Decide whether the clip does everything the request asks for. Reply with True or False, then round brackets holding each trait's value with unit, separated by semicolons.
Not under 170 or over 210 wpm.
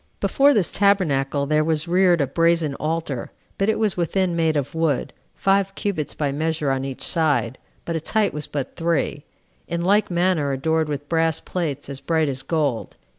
True (180 wpm)